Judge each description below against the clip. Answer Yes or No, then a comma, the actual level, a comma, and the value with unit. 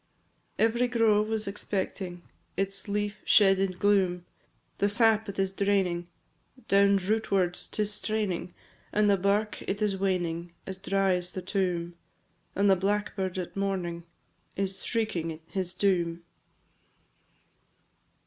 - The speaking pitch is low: No, high, 195 Hz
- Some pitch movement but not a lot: No, narrow, 2.3 semitones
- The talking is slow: Yes, slow, 130 wpm